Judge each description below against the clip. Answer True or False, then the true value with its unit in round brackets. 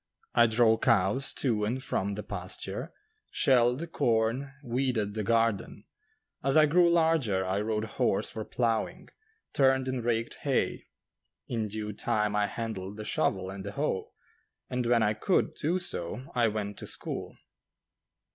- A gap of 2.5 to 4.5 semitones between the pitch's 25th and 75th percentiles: True (3.8 semitones)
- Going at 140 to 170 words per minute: True (150 wpm)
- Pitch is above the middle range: False (115 Hz)